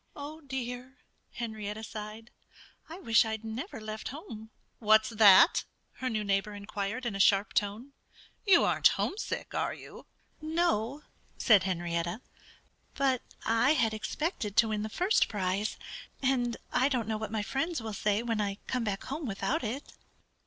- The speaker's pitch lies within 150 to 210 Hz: No, high, 225 Hz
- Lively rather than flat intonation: No, average, 4.1 semitones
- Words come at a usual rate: Yes, average, 155 wpm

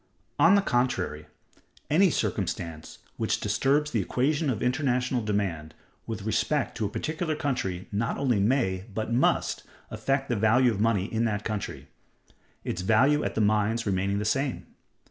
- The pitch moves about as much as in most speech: Yes, average, 5.0 semitones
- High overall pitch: No, low, 115 Hz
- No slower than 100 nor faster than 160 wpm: Yes, average, 150 wpm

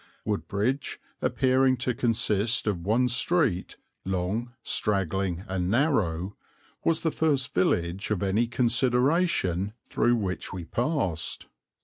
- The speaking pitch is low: Yes, low, 110 Hz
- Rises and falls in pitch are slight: No, average, 5.2 semitones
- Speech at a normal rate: No, slow, 110 wpm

